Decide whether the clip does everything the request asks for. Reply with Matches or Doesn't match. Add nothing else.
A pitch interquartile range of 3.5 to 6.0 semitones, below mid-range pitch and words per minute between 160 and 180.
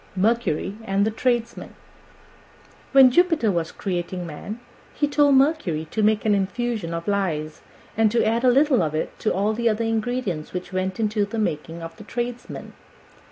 Doesn't match